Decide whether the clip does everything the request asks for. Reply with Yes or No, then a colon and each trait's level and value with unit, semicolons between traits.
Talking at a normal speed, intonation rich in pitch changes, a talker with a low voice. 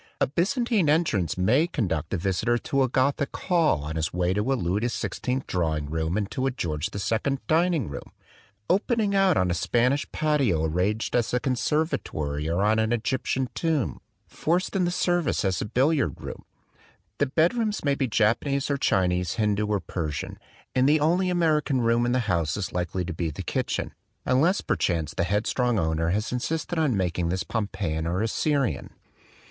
Yes: average, 180 wpm; wide, 8.8 semitones; low, 120 Hz